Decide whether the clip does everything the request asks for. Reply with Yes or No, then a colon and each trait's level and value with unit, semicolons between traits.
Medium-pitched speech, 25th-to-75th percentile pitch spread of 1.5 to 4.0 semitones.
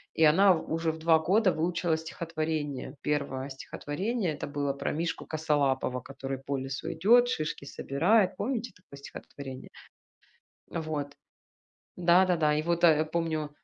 Yes: medium, 155 Hz; average, 3.3 semitones